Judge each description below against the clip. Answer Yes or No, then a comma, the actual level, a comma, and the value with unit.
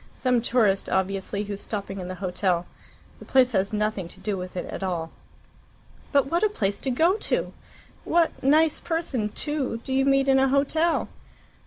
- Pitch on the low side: No, high, 230 Hz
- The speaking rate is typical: Yes, average, 180 wpm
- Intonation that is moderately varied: No, wide, 6.1 semitones